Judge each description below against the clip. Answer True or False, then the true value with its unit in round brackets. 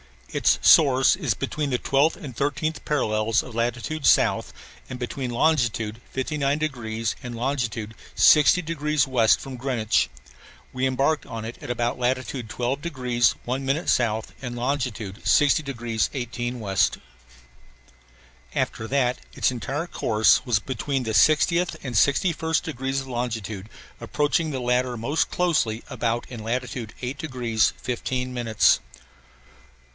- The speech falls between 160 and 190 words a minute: False (135 wpm)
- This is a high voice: False (125 Hz)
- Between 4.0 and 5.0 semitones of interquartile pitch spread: False (3.4 semitones)